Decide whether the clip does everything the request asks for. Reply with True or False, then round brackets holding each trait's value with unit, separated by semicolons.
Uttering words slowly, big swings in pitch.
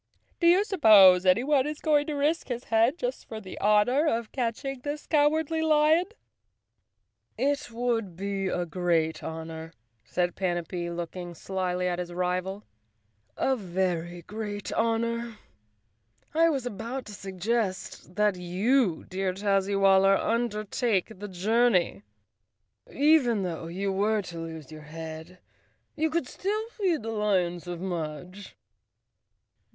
True (130 wpm; 5.9 semitones)